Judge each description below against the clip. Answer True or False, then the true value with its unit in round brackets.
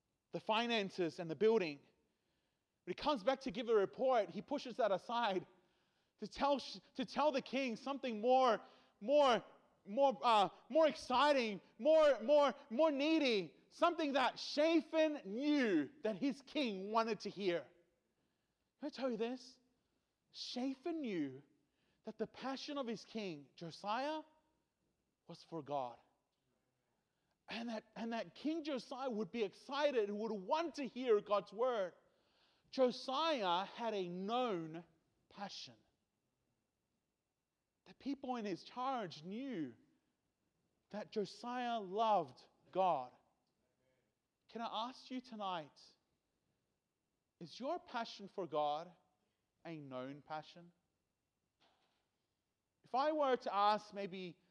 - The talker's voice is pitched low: False (225 Hz)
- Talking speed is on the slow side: True (120 wpm)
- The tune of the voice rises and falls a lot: True (6.3 semitones)